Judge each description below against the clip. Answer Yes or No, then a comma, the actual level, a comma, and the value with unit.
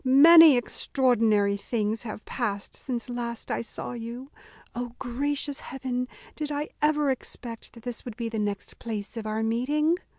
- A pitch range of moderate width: Yes, average, 3.4 semitones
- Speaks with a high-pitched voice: Yes, high, 245 Hz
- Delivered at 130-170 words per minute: Yes, average, 160 wpm